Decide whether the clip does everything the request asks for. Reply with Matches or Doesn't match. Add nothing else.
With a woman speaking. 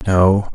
Doesn't match